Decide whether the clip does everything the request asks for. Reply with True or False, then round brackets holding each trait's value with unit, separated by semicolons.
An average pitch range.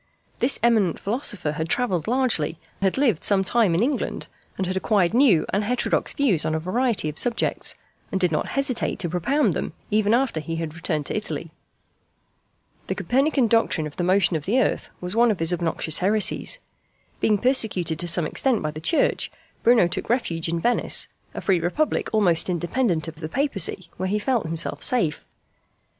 False (6.3 semitones)